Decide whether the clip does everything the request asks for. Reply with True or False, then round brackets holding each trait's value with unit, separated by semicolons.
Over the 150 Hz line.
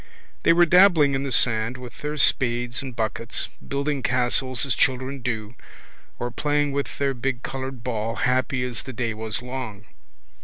False (130 Hz)